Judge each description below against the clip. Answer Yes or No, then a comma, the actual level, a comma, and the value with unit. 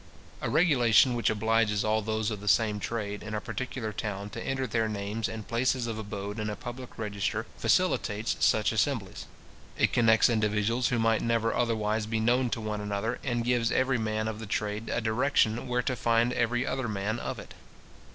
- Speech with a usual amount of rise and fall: No, narrow, 2.0 semitones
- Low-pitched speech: Yes, low, 110 Hz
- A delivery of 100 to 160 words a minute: No, average, 190 wpm